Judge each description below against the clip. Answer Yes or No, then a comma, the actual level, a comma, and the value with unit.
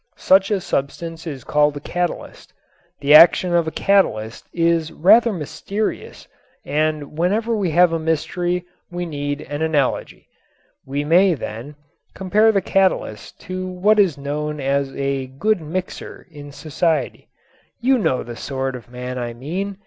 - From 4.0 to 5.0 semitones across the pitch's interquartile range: Yes, average, 4.7 semitones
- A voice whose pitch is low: No, medium, 160 Hz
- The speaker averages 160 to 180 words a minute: No, average, 150 wpm